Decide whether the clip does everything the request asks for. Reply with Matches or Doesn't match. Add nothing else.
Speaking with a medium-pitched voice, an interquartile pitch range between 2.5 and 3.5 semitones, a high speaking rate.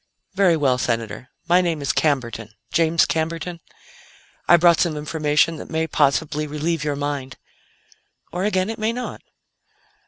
Doesn't match